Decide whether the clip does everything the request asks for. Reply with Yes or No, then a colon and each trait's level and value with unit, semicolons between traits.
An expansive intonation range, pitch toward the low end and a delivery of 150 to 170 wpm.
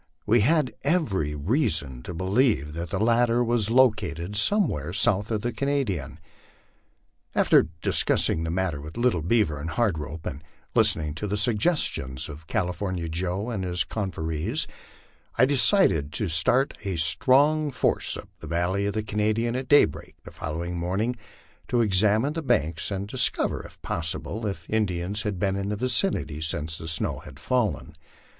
Yes: wide, 6.4 semitones; low, 100 Hz; average, 165 wpm